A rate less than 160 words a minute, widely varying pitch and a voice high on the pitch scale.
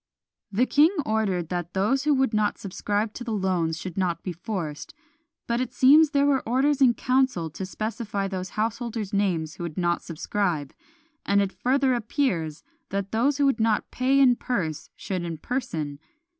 No: average, 175 wpm; wide, 6.1 semitones; high, 210 Hz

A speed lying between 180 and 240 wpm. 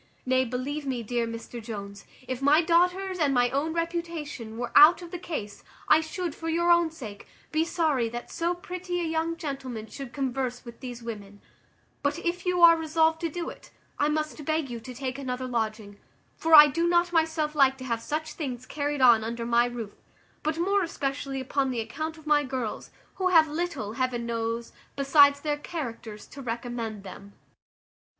Yes: average, 185 wpm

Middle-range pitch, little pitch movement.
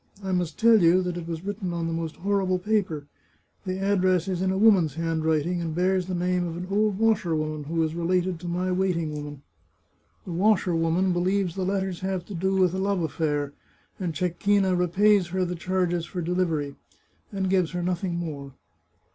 Yes: medium, 180 Hz; narrow, 2.3 semitones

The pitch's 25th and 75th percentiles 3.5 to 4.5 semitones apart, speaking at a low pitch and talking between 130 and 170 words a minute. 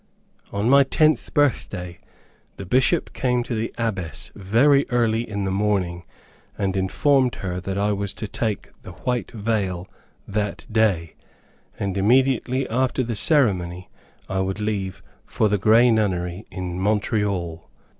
Yes: average, 4.1 semitones; low, 105 Hz; average, 140 wpm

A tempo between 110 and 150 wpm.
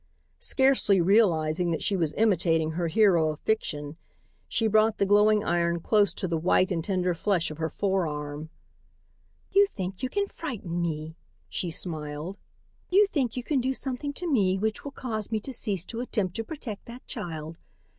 No: average, 175 wpm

